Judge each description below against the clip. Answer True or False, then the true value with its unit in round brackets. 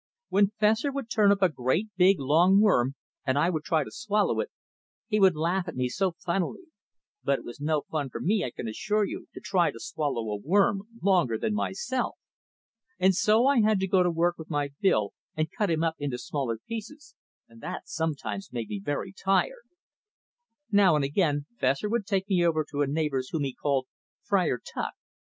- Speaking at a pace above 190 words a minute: True (200 wpm)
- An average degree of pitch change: False (5.9 semitones)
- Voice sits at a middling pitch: True (170 Hz)